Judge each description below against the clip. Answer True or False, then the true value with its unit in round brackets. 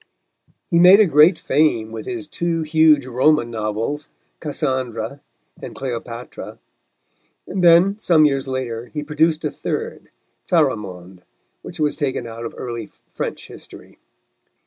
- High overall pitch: False (145 Hz)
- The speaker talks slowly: True (130 wpm)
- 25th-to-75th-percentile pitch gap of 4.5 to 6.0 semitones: True (5.5 semitones)